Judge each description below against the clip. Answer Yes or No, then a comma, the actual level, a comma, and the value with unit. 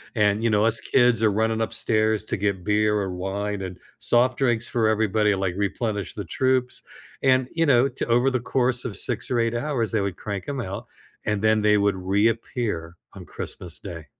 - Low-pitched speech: Yes, low, 110 Hz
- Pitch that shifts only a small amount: No, average, 3.1 semitones